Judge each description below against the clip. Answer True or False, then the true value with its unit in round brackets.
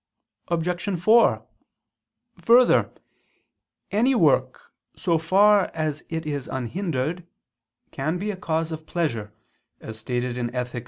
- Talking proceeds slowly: True (115 wpm)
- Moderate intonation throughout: False (6.2 semitones)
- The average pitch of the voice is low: False (160 Hz)